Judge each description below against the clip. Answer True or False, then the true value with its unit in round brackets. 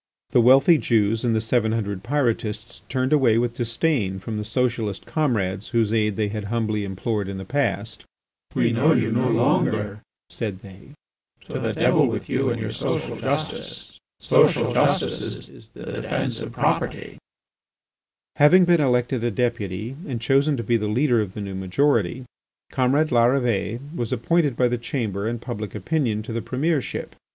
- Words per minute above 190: False (165 wpm)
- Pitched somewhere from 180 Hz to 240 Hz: False (115 Hz)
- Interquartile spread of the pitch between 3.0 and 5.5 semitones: True (3.4 semitones)